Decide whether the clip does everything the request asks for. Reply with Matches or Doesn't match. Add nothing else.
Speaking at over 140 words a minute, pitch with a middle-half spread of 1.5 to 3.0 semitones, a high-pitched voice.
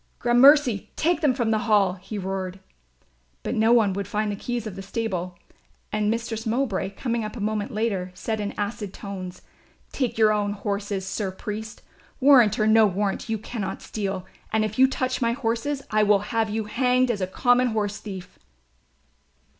Matches